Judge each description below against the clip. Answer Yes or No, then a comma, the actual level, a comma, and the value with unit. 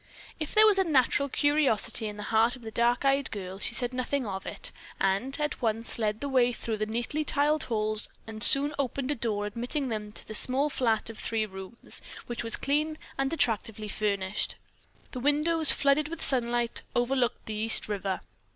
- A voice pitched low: No, high, 240 Hz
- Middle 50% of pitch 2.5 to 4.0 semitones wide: No, average, 4.5 semitones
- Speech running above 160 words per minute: Yes, average, 190 wpm